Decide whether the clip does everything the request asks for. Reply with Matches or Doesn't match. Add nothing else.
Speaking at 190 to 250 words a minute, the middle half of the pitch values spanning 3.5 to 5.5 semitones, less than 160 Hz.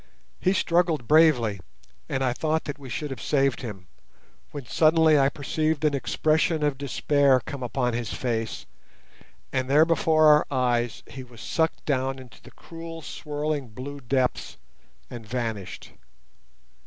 Doesn't match